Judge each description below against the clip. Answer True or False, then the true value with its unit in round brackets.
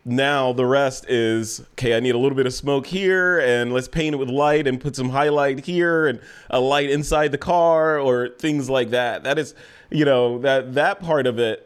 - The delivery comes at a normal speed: False (220 wpm)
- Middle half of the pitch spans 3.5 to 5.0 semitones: False (3.0 semitones)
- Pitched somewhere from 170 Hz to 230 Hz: False (140 Hz)